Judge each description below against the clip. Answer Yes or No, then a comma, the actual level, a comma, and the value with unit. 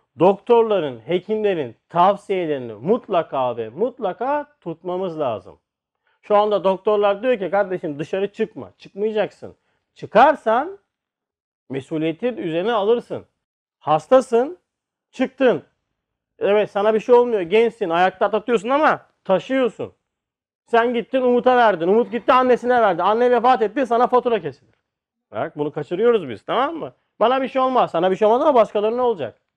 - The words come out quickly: No, average, 130 wpm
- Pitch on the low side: No, high, 215 Hz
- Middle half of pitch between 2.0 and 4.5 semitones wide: No, average, 5.1 semitones